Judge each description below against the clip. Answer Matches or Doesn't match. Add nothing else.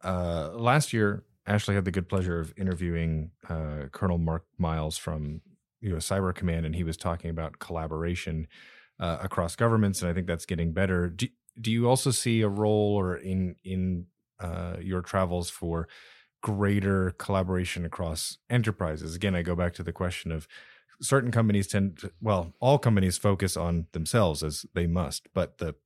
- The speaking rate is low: Doesn't match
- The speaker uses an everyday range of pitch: Matches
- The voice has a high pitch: Doesn't match